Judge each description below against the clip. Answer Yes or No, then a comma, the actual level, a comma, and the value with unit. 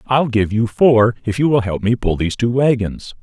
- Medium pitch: No, low, 115 Hz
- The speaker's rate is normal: No, fast, 240 wpm